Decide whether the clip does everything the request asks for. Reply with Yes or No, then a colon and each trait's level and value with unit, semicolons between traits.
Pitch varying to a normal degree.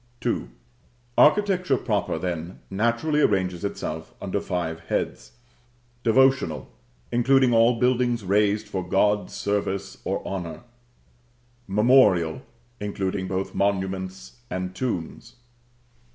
Yes: average, 4.3 semitones